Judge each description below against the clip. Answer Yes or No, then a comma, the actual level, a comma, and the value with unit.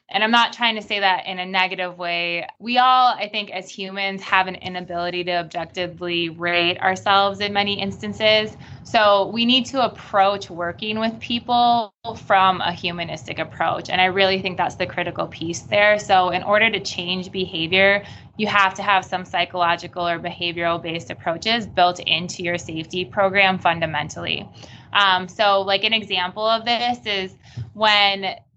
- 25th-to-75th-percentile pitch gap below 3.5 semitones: Yes, average, 3.0 semitones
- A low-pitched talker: No, high, 190 Hz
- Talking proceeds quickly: No, average, 165 wpm